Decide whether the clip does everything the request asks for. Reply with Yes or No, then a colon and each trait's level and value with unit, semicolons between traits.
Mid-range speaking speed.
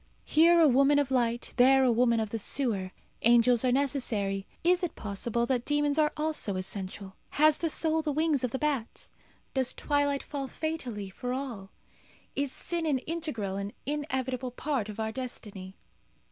Yes: average, 170 wpm